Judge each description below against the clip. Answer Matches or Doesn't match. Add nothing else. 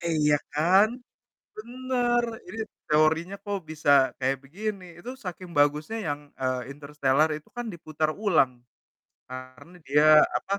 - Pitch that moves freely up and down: Matches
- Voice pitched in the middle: Matches